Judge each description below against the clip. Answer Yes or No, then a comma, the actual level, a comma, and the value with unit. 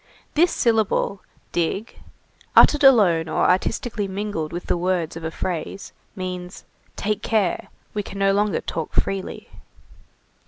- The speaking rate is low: Yes, slow, 130 wpm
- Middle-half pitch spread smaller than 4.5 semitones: Yes, average, 3.2 semitones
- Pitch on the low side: No, high, 195 Hz